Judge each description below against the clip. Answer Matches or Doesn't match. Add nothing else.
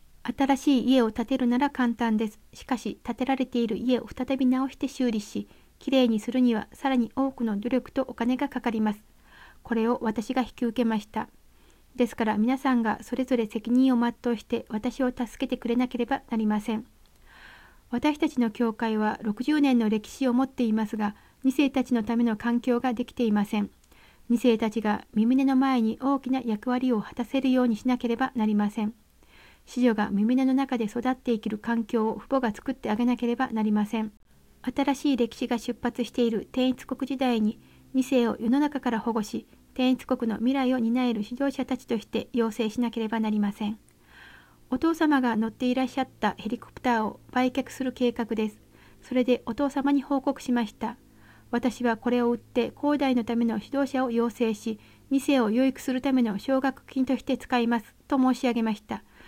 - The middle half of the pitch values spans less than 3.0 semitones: Matches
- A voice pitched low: Doesn't match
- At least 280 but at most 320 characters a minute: Doesn't match